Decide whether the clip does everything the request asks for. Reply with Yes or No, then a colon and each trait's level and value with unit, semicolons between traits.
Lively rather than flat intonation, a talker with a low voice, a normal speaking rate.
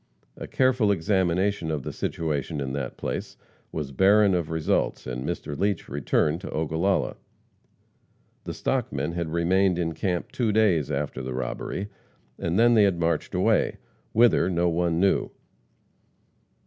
No: average, 4.3 semitones; very low, 85 Hz; average, 145 wpm